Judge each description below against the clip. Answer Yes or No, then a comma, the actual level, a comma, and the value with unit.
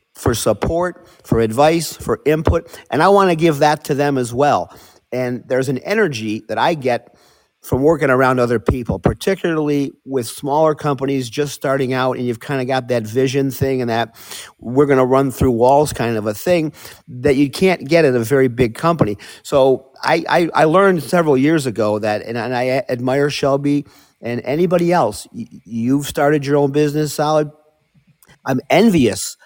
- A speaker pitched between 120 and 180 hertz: Yes, medium, 140 Hz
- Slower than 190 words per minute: Yes, average, 180 wpm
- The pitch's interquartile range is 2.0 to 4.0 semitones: Yes, average, 3.4 semitones